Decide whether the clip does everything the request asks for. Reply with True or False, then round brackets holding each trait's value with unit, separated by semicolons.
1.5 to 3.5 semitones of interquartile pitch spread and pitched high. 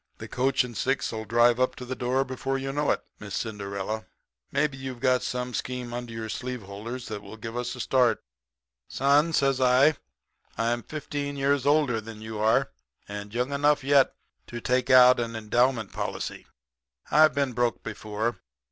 False (3.1 semitones; 125 Hz)